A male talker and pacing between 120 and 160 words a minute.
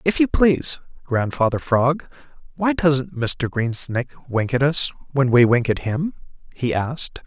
Yes: male; average, 155 wpm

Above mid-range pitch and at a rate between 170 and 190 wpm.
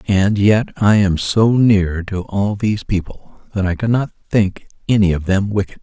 No: low, 100 Hz; average, 185 wpm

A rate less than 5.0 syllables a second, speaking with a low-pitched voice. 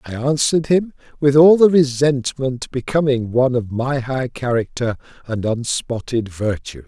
Yes: 4.4 syllables/s; low, 130 Hz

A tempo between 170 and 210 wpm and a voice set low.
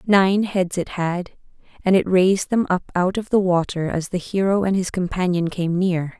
No: fast, 205 wpm; medium, 185 Hz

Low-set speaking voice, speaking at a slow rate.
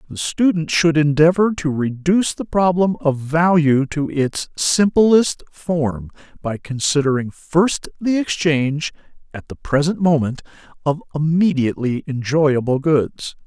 No: medium, 155 Hz; slow, 120 wpm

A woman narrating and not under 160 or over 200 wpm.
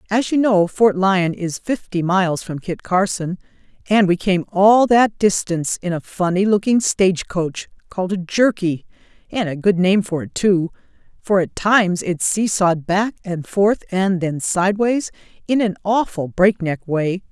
Yes: female; average, 170 wpm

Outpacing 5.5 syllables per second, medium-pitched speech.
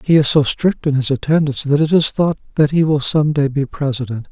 Yes: 5.7 syllables/s; medium, 145 Hz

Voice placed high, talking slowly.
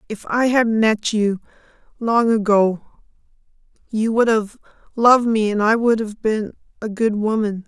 Yes: high, 220 Hz; slow, 115 wpm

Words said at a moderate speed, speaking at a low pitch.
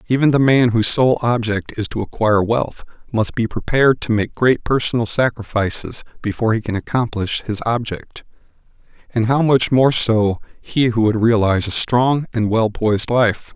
Yes: average, 175 wpm; low, 115 Hz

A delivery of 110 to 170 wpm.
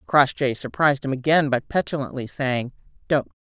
Yes: average, 140 wpm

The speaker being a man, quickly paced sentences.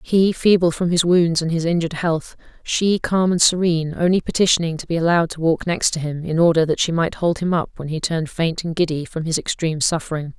No: female; fast, 235 wpm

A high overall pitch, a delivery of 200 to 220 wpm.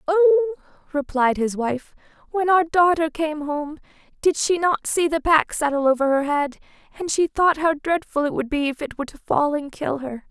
Yes: very high, 305 Hz; fast, 205 wpm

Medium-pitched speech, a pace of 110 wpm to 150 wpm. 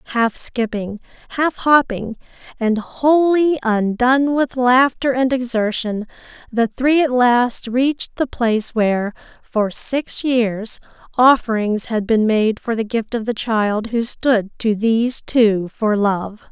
No: high, 235 Hz; average, 140 wpm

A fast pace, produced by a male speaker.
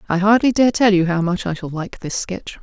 No: fast, 275 wpm; female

